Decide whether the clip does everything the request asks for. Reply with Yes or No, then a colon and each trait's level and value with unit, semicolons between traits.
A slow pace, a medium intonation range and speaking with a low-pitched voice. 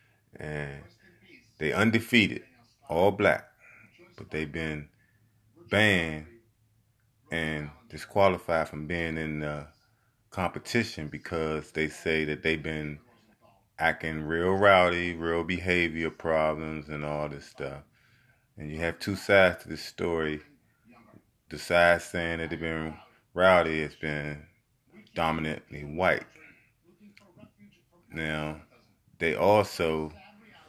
Yes: slow, 105 wpm; average, 4.6 semitones; very low, 80 Hz